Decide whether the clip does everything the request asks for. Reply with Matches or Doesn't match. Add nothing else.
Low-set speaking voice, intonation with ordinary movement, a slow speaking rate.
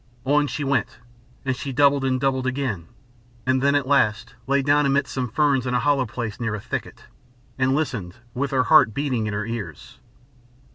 Doesn't match